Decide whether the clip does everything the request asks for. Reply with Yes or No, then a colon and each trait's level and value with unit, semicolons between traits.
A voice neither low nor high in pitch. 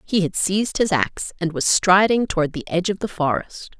Yes: medium, 180 Hz